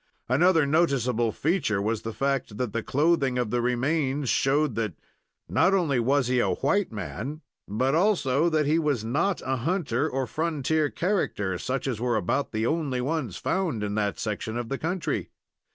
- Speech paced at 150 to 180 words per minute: Yes, average, 175 wpm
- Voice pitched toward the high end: No, low, 135 Hz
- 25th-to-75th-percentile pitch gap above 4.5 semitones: Yes, average, 5.2 semitones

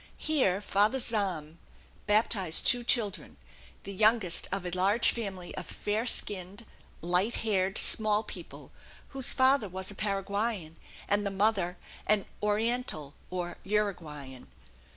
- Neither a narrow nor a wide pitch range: Yes, average, 3.1 semitones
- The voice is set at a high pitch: Yes, high, 200 Hz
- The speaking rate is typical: No, slow, 125 wpm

